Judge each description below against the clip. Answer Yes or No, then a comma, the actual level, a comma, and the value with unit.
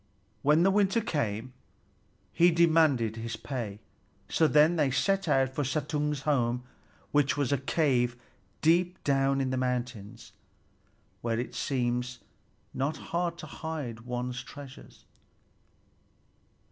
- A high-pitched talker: No, low, 135 Hz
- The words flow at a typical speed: No, slow, 120 wpm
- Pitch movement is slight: No, average, 4.3 semitones